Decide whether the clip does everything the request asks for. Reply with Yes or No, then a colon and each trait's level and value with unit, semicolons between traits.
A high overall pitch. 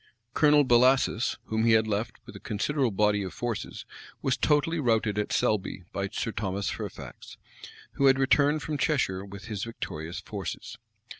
No: low, 115 Hz